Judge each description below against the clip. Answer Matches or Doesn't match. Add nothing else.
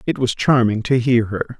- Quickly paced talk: Matches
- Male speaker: Matches